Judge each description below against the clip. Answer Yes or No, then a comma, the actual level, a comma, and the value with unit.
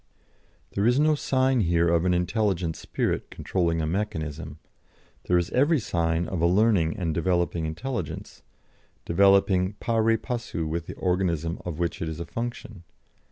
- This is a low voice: Yes, very low, 90 Hz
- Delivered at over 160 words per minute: No, average, 155 wpm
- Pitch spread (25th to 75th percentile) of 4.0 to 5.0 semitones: Yes, average, 4.7 semitones